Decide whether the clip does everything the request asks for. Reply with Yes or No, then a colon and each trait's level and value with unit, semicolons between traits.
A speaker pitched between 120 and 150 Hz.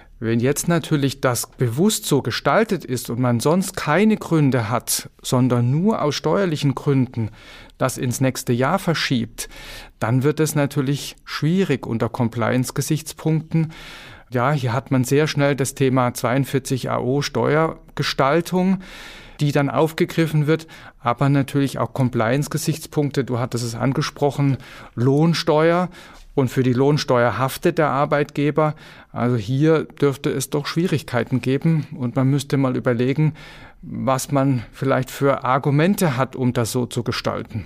Yes: medium, 140 Hz